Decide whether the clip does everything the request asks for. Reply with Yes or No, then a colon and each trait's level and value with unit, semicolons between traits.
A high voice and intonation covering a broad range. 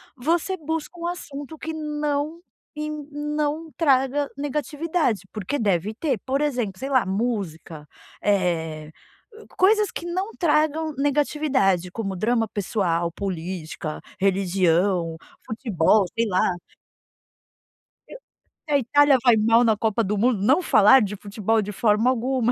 Yes: high, 245 Hz; wide, 7.1 semitones